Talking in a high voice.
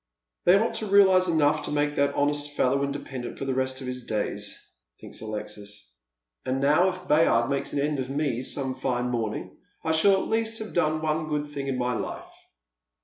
No: medium, 140 Hz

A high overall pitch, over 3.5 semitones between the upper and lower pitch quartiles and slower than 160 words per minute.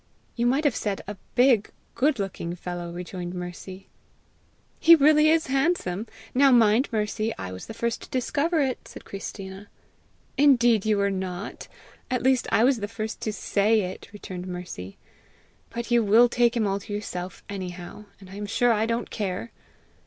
No: high, 215 Hz; average, 4.3 semitones; average, 175 wpm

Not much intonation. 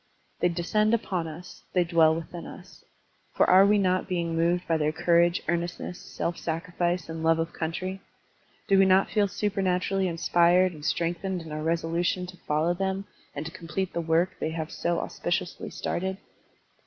Yes: narrow, 2.1 semitones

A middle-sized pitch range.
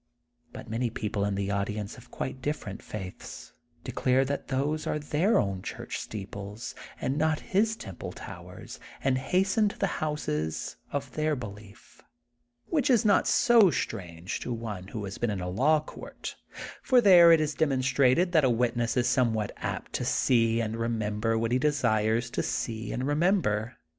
No: wide, 6.2 semitones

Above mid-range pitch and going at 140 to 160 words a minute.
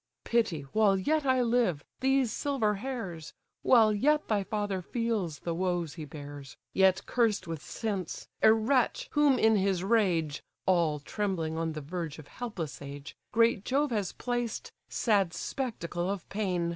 Yes: high, 200 Hz; average, 155 wpm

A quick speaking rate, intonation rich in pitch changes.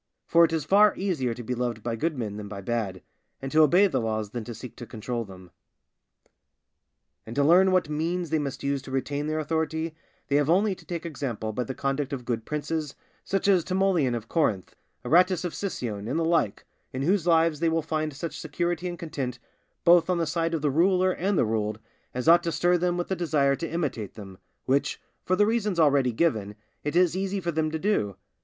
Yes: fast, 220 wpm; wide, 5.7 semitones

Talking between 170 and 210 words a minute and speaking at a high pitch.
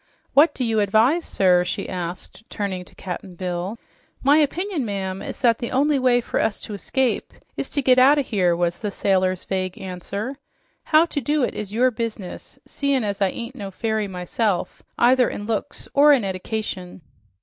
Yes: average, 185 wpm; high, 215 Hz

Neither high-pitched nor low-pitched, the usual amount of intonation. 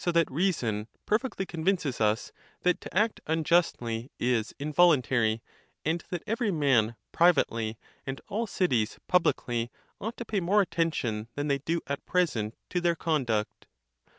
No: medium, 155 Hz; wide, 7.1 semitones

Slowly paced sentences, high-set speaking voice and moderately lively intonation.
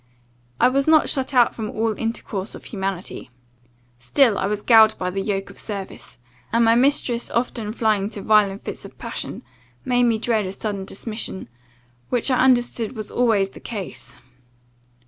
No: average, 165 wpm; high, 220 Hz; average, 3.3 semitones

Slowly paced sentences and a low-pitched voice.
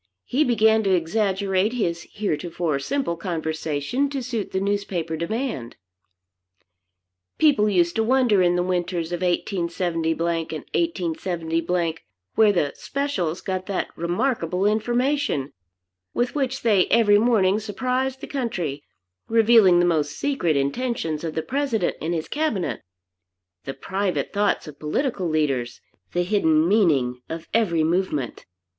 No: slow, 130 wpm; medium, 185 Hz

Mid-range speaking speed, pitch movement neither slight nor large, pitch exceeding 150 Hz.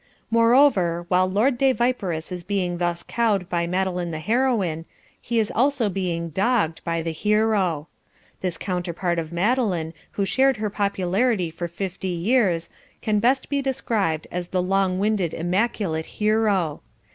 Yes: average, 145 wpm; average, 4.5 semitones; high, 190 Hz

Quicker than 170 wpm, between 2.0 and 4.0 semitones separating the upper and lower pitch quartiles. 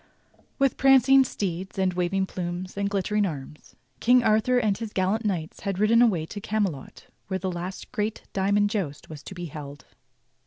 Yes: average, 180 wpm; average, 3.4 semitones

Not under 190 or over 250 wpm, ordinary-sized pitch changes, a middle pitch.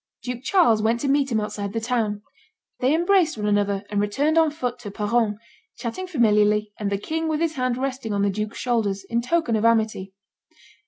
No: average, 200 wpm; average, 4.7 semitones; high, 230 Hz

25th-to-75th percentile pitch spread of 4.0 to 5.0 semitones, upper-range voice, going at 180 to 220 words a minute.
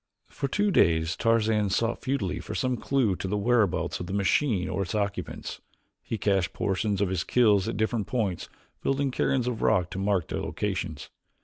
No: average, 4.3 semitones; low, 105 Hz; average, 185 wpm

